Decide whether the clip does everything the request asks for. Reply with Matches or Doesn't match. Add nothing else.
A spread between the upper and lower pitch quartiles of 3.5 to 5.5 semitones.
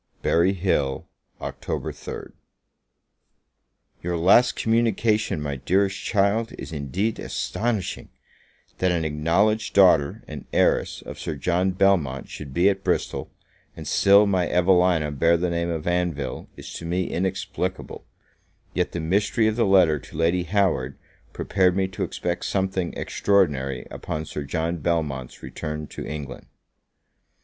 Matches